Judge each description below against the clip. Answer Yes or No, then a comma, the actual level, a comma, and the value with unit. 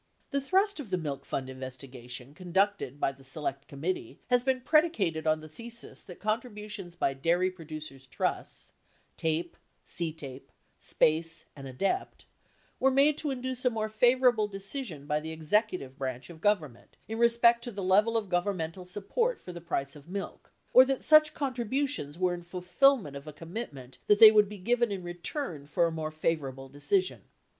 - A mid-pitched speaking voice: Yes, medium, 180 Hz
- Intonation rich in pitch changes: Yes, wide, 7.6 semitones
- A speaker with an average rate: Yes, average, 170 wpm